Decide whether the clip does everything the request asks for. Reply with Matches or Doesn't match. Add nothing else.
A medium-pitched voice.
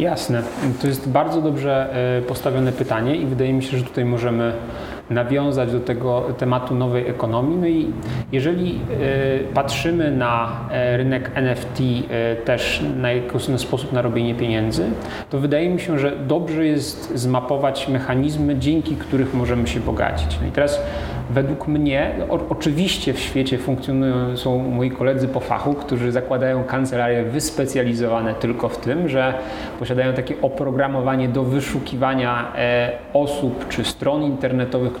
Doesn't match